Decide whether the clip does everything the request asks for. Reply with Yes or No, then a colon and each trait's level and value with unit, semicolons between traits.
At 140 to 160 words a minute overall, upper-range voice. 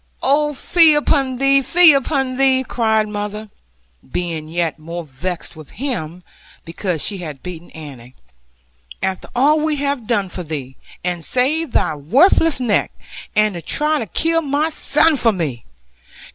Yes: average, 150 wpm; high, 220 Hz